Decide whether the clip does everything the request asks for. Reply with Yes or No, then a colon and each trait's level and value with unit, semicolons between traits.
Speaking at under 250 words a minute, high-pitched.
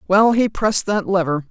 Yes: average, 200 wpm; high, 195 Hz